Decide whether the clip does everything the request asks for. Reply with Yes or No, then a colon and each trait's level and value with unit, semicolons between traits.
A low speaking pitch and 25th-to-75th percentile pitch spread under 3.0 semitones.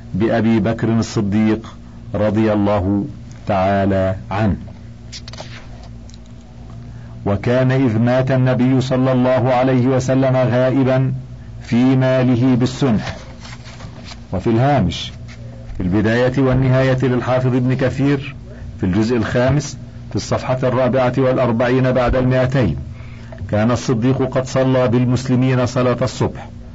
Yes: low, 125 Hz; narrow, 2.4 semitones